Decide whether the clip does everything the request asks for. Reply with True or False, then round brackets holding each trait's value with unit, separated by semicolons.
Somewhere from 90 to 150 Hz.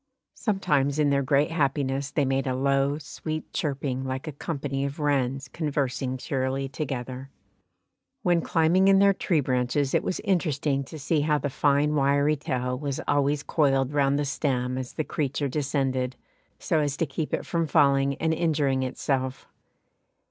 True (140 Hz)